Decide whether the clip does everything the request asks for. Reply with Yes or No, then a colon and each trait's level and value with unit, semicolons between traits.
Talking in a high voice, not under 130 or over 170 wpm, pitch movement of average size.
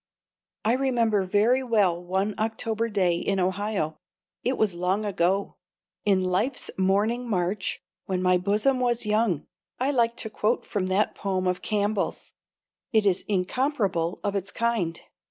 Yes: high, 205 Hz; average, 145 wpm; average, 3.6 semitones